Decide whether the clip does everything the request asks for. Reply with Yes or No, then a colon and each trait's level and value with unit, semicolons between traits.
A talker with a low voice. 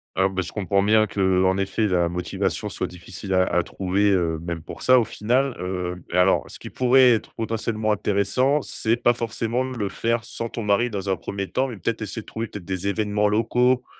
Yes: low, 105 Hz